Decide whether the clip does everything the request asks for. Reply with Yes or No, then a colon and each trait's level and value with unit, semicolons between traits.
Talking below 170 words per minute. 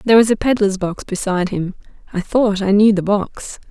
No: fast, 210 wpm